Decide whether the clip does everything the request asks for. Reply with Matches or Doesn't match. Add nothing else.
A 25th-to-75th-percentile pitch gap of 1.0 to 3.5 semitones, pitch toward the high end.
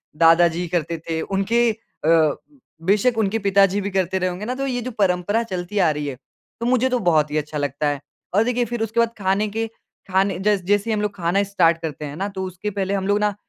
Doesn't match